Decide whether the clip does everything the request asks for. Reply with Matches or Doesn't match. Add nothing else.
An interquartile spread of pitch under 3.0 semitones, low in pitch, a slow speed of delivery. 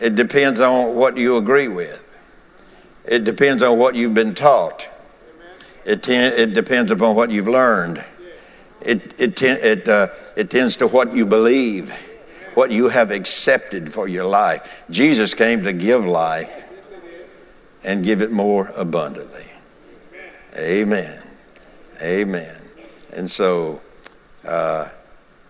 Matches